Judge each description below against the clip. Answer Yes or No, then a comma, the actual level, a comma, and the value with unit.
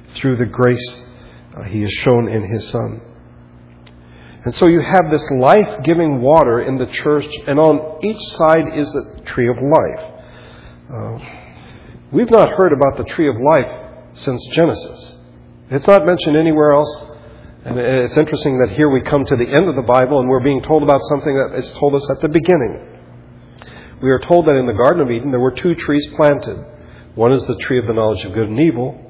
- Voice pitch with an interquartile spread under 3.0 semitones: No, average, 4.5 semitones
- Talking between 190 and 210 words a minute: Yes, average, 200 wpm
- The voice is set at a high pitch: No, low, 135 Hz